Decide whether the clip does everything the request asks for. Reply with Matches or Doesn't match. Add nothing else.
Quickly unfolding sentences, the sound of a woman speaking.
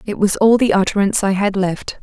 Matches